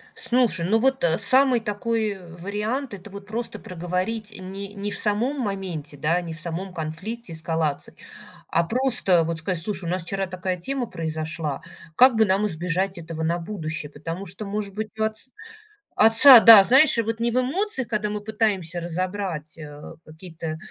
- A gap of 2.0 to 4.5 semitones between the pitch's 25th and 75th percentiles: No, average, 4.9 semitones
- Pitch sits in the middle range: No, high, 195 Hz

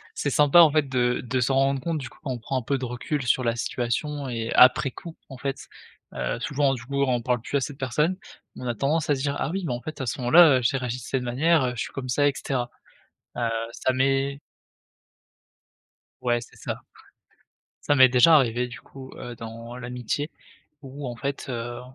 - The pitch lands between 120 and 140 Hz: Yes, low, 130 Hz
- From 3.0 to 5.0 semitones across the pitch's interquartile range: No, narrow, 2.6 semitones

